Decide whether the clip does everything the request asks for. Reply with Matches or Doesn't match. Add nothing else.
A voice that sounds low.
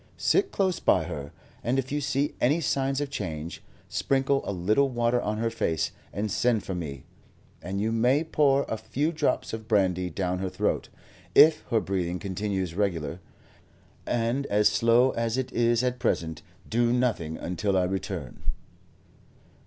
Matches